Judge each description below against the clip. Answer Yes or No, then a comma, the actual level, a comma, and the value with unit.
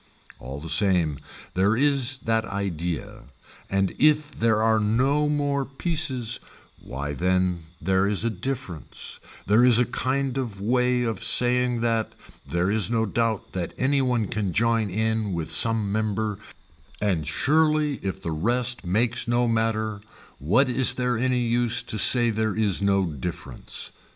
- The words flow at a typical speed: Yes, average, 150 wpm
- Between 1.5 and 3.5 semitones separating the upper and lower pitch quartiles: No, average, 4.3 semitones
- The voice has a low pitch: Yes, low, 110 Hz